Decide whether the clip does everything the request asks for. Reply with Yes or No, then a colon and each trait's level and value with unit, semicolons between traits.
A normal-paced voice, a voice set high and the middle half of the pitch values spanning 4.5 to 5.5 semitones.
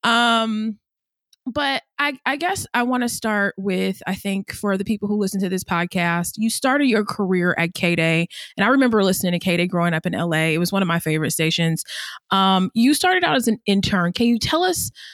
No: fast, 215 wpm; high, 200 Hz; average, 5.2 semitones